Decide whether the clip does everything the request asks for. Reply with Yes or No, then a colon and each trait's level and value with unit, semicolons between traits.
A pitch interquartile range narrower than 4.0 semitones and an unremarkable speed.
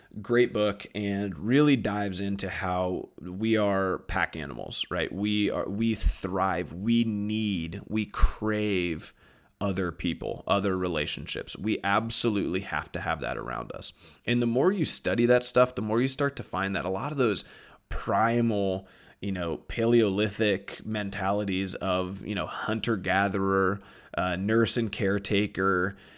Yes: average, 2.7 semitones; average, 145 wpm